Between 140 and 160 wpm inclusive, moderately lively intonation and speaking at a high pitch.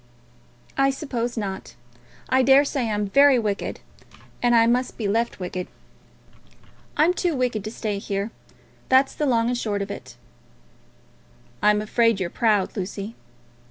Yes: average, 145 wpm; average, 4.0 semitones; high, 230 Hz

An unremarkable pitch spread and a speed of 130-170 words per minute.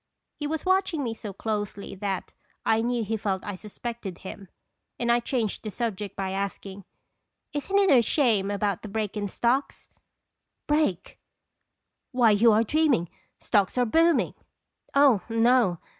Yes: average, 4.1 semitones; average, 160 wpm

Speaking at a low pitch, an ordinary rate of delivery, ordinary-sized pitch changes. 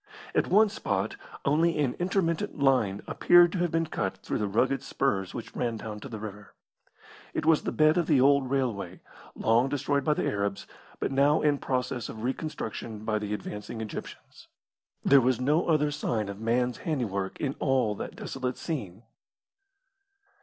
No: low, 130 Hz; average, 170 wpm; wide, 5.7 semitones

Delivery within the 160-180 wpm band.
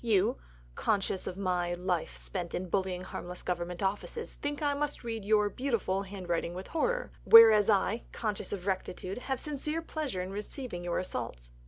Yes: average, 170 wpm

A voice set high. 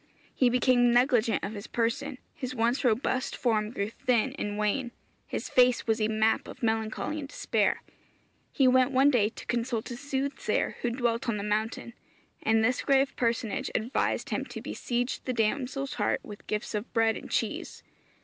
Yes: high, 240 Hz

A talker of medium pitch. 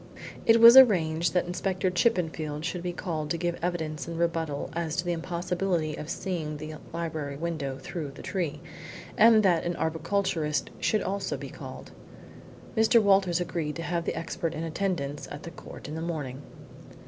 Yes: medium, 170 Hz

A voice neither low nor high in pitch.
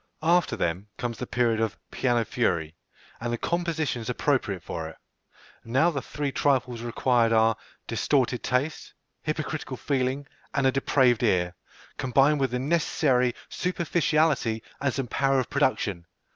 No: low, 130 Hz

